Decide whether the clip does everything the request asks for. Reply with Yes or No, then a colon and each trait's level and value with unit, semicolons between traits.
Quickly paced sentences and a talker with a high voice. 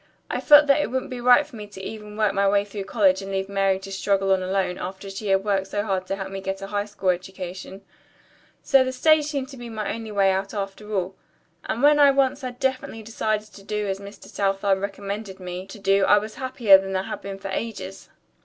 Yes: fast, 240 wpm; high, 200 Hz